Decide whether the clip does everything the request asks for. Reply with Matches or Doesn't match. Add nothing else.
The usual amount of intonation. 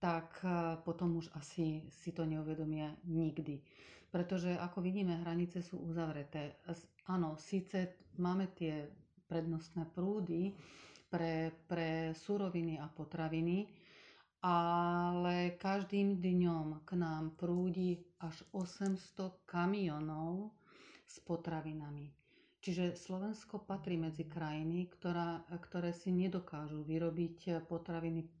Doesn't match